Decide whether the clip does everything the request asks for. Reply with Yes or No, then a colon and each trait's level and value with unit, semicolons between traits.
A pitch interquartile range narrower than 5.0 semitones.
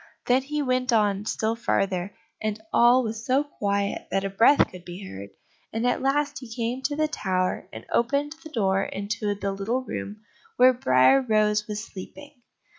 Yes: average, 4.5 semitones